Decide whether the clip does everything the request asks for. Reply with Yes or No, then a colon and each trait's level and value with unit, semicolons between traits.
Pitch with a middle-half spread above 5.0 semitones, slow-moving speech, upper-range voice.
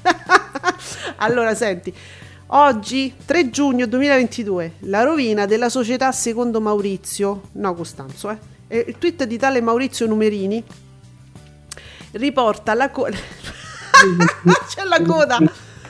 Yes: wide, 5.6 semitones; slow, 100 wpm; high, 225 Hz